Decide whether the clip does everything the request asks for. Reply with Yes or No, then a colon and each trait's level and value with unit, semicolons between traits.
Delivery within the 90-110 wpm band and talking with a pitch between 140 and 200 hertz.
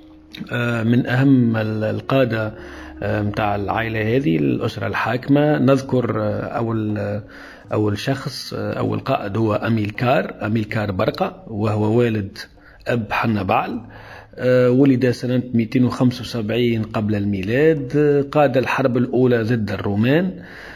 No: average, 95 wpm; low, 115 Hz